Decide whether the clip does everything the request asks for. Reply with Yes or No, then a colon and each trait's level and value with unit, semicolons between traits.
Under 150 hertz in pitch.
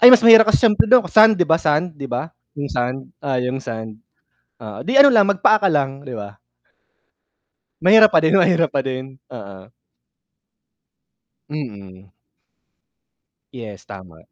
Yes: medium, 140 Hz